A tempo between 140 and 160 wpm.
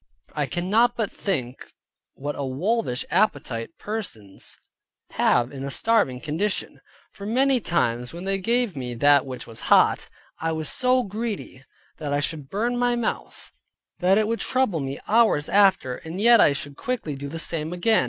No: average, 170 wpm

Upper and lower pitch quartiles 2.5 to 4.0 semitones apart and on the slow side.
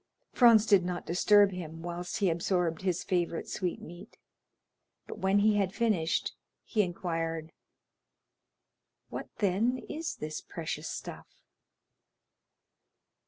Yes: average, 3.3 semitones; slow, 110 wpm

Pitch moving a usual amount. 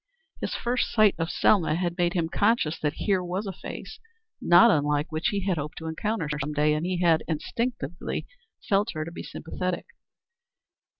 Yes: average, 4.1 semitones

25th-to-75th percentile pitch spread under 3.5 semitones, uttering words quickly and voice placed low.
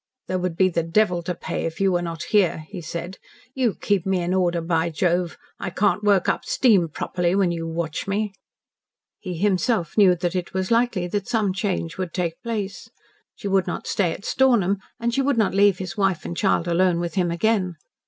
No: average, 2.9 semitones; fast, 210 wpm; medium, 185 Hz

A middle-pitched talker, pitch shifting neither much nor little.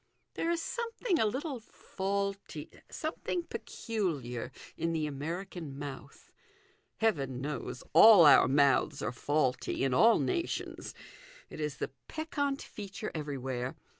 No: medium, 165 Hz; wide, 8.6 semitones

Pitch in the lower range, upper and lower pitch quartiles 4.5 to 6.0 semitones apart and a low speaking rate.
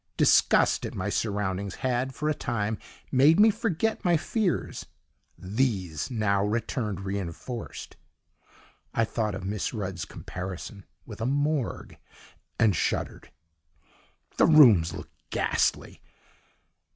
Yes: low, 110 Hz; wide, 5.5 semitones; slow, 115 wpm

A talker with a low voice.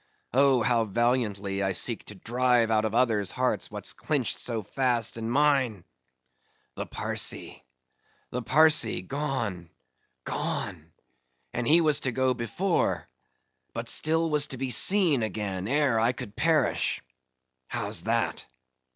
Yes: low, 115 Hz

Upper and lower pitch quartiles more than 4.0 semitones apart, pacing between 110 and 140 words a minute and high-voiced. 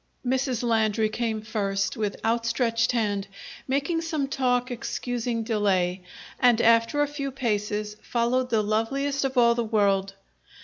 No: average, 3.1 semitones; slow, 135 wpm; high, 230 Hz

